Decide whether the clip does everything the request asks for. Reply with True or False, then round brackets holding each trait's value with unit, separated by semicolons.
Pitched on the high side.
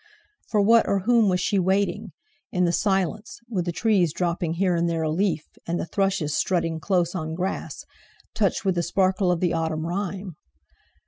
False (180 Hz)